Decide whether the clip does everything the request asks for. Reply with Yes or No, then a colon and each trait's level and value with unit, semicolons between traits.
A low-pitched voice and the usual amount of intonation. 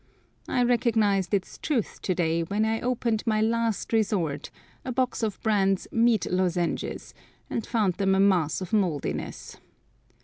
No: high, 210 Hz; average, 3.6 semitones